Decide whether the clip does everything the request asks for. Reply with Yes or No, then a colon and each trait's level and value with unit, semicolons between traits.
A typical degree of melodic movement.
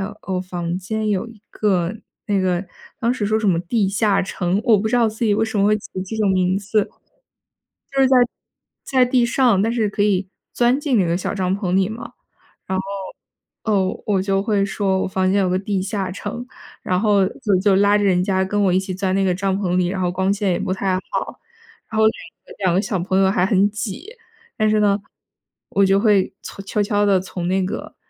No: narrow, 2.2 semitones